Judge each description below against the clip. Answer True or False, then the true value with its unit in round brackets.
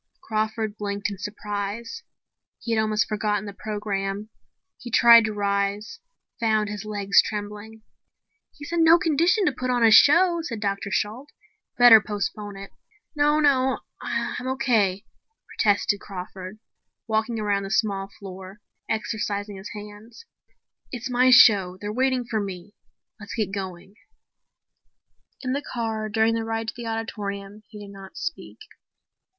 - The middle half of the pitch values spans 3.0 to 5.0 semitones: False (2.6 semitones)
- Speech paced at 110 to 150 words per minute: True (145 wpm)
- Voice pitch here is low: False (215 Hz)